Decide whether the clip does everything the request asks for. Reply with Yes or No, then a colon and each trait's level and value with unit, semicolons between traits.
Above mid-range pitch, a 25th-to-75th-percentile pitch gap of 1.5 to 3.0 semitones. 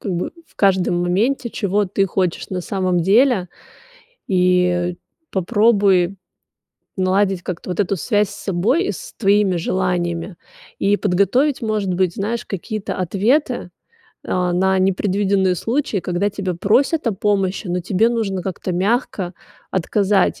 Yes: high, 195 Hz; narrow, 2.5 semitones